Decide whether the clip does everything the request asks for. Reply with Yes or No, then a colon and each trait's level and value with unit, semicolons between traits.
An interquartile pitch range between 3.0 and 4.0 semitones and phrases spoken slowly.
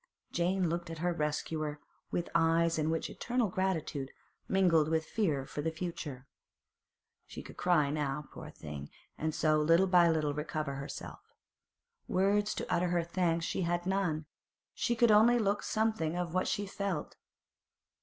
No: average, 3.4 semitones; average, 155 wpm